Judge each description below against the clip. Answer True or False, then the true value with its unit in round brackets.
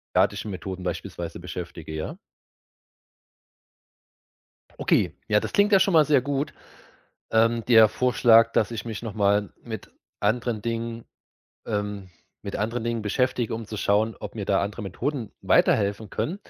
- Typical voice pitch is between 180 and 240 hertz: False (110 Hz)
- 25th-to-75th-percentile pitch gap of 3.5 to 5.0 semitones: False (2.8 semitones)